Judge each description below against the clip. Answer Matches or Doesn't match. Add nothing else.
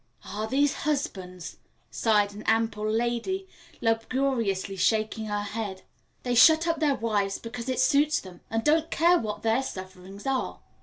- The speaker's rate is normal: Matches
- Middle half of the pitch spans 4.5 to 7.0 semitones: Matches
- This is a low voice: Doesn't match